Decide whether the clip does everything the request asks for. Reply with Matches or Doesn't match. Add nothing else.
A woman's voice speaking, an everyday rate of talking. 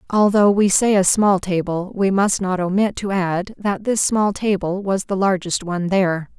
Matches